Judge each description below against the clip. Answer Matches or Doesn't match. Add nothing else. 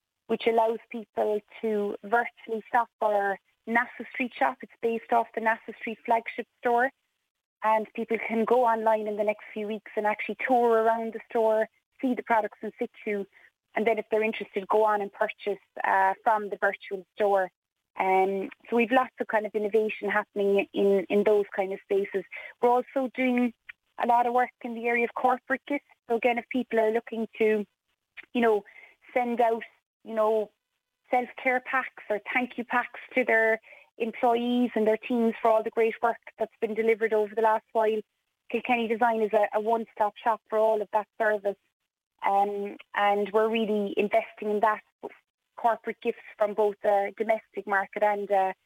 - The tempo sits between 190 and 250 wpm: Doesn't match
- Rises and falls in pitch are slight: Matches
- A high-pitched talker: Matches